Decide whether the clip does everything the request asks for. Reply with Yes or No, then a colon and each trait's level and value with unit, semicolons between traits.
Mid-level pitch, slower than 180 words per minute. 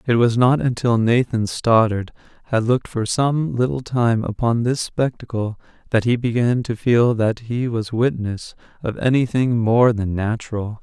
No: low, 115 Hz; average, 165 wpm